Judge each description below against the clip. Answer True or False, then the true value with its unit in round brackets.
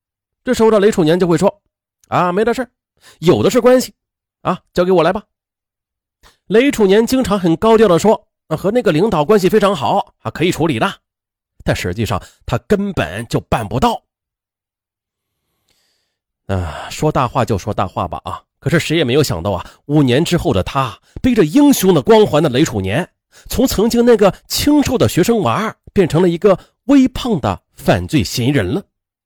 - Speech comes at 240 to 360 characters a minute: True (255 characters per minute)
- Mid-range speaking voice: True (180 Hz)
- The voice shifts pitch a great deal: True (8.9 semitones)